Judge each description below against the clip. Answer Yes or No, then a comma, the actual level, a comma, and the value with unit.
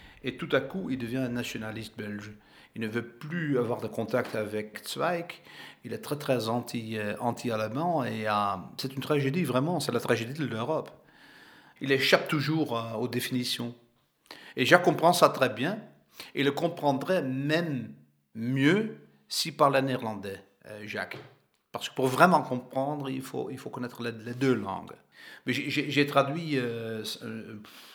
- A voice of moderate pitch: No, low, 125 Hz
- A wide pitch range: No, average, 4.3 semitones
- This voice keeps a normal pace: Yes, average, 170 wpm